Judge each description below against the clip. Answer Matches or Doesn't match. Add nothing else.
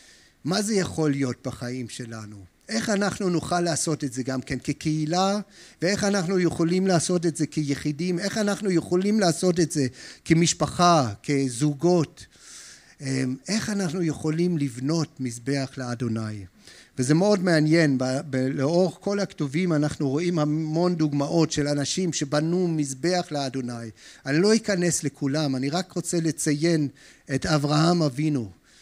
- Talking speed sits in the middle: Matches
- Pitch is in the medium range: Matches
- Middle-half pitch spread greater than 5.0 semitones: Doesn't match